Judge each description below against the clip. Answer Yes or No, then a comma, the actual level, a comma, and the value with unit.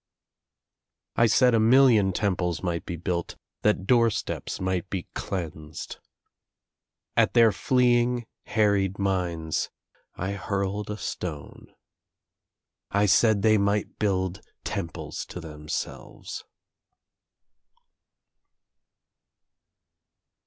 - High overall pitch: No, low, 100 Hz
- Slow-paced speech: Yes, slow, 90 wpm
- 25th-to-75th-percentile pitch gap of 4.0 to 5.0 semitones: No, average, 3.6 semitones